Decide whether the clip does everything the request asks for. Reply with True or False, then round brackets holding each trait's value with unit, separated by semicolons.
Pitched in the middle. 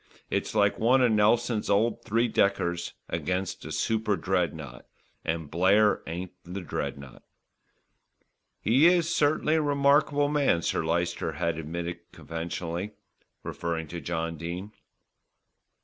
False (95 Hz)